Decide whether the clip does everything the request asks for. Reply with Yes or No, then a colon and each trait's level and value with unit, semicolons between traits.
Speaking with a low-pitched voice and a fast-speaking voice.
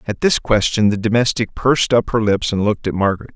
Yes: low, 110 Hz; fast, 230 wpm